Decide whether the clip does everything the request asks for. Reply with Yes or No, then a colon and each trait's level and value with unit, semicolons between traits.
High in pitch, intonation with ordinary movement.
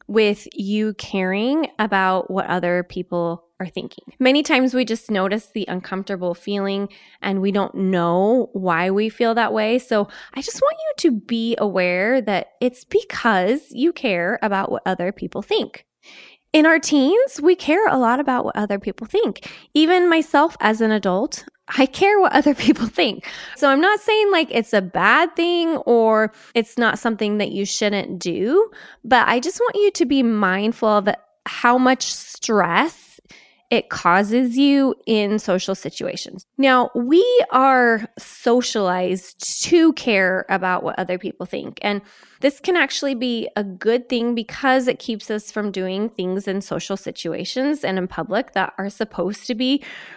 No: high, 225 Hz; wide, 5.9 semitones